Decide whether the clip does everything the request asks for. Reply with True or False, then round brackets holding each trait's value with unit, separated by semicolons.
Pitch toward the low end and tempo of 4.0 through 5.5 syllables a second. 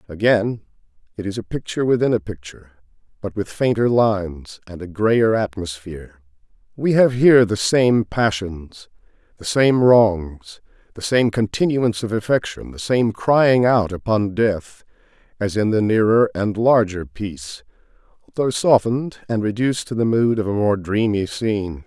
True (105 Hz; 4.6 syllables/s)